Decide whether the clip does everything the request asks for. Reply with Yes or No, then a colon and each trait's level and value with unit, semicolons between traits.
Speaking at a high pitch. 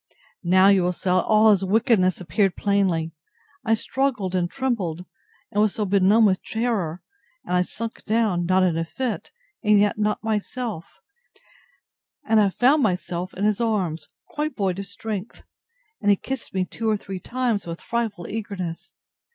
Yes: high, 200 Hz